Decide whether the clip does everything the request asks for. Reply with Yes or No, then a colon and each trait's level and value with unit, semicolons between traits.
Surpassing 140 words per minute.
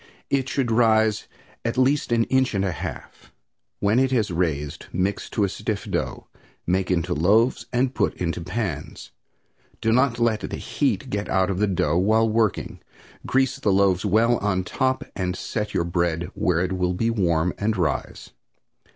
Yes: average, 175 wpm